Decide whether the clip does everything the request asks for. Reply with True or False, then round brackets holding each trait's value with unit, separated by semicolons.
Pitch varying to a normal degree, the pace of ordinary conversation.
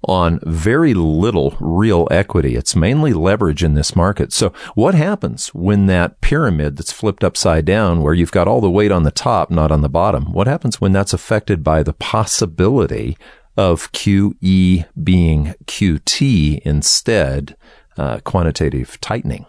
True (4.0 semitones; 155 wpm)